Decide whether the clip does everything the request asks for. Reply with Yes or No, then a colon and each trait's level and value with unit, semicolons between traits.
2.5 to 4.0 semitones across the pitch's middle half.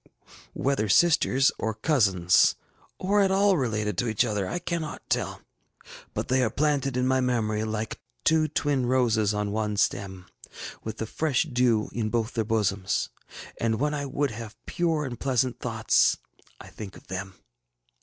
No: average, 4.7 semitones